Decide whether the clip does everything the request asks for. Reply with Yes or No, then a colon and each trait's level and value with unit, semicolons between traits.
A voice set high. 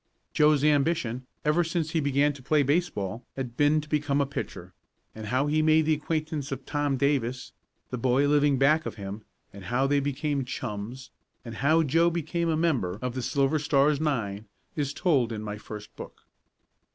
No: medium, 140 Hz